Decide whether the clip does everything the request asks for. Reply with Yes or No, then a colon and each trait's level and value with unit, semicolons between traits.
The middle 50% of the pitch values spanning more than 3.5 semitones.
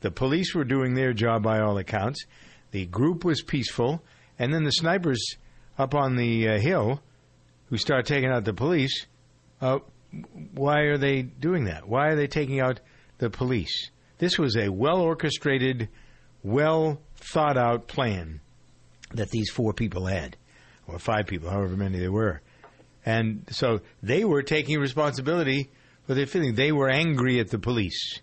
Yes: average, 4.6 semitones